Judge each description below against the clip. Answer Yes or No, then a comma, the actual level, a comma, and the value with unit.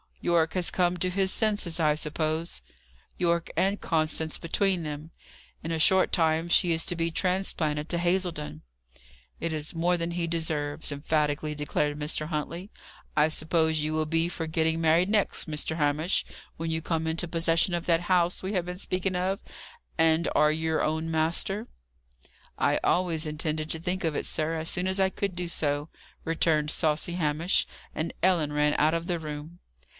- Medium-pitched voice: Yes, medium, 165 Hz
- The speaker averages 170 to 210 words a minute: Yes, average, 175 wpm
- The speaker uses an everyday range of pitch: No, narrow, 2.2 semitones